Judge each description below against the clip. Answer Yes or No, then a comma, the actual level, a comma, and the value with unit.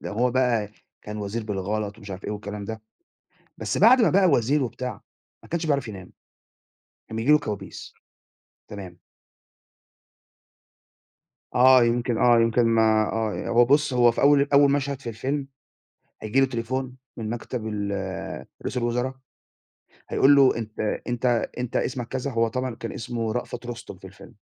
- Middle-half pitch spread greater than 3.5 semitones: No, average, 3.2 semitones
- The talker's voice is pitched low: Yes, low, 120 Hz